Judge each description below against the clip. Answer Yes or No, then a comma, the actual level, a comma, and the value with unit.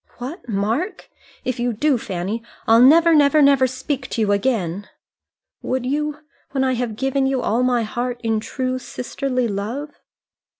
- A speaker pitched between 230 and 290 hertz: Yes, very high, 250 Hz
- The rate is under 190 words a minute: Yes, average, 160 wpm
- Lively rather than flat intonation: No, average, 3.4 semitones